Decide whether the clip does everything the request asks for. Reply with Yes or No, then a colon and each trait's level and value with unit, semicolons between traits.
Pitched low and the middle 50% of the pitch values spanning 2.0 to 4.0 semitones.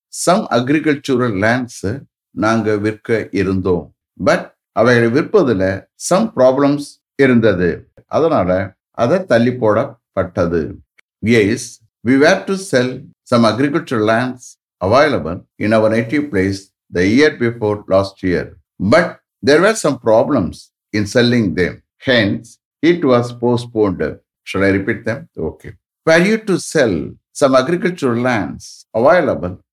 No: low, 120 Hz; average, 4.5 semitones